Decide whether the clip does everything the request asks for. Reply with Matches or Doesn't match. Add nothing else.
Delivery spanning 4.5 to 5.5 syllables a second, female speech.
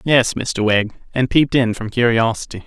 Doesn't match